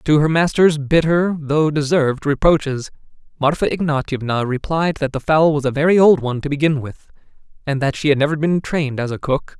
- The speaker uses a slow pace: No, average, 195 wpm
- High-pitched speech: No, medium, 150 Hz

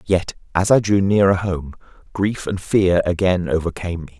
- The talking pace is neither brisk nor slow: Yes, average, 170 wpm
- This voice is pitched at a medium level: No, very low, 90 Hz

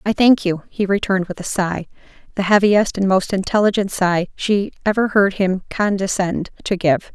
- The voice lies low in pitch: No, high, 195 Hz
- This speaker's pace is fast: No, average, 170 wpm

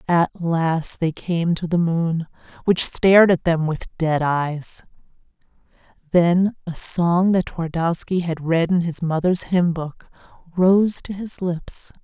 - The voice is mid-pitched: Yes, medium, 170 Hz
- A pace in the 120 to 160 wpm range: Yes, average, 150 wpm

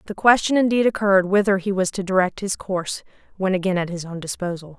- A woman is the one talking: Yes, female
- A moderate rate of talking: No, fast, 215 wpm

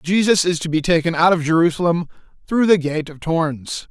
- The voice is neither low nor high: Yes, medium, 165 Hz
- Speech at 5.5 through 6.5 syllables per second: Yes, 5.6 syllables/s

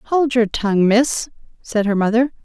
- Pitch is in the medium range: No, high, 230 Hz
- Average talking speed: Yes, average, 170 wpm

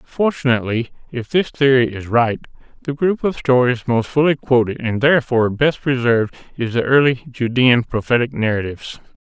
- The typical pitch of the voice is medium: No, low, 125 Hz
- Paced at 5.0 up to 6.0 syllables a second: Yes, 5.4 syllables/s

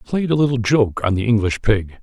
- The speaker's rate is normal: No, fast, 235 wpm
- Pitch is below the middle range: Yes, low, 115 Hz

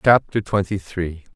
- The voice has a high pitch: No, very low, 95 Hz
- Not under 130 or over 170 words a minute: Yes, slow, 135 wpm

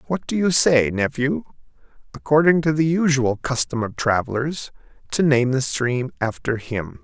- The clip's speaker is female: No, male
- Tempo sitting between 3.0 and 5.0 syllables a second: Yes, 4.5 syllables/s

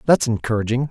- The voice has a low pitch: Yes, low, 125 Hz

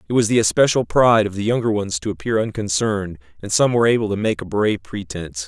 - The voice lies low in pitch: Yes, low, 105 Hz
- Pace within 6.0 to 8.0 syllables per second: Yes, 6.7 syllables/s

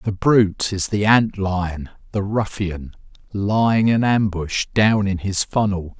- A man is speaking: Yes, male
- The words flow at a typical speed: Yes, average, 150 wpm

